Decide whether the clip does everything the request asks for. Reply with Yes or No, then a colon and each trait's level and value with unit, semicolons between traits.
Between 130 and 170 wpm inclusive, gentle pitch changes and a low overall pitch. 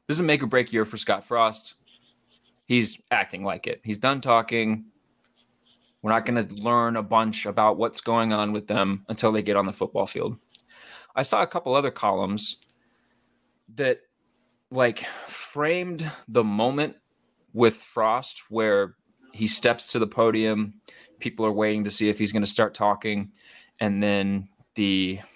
Yes: average, 165 wpm; narrow, 2.3 semitones; low, 110 Hz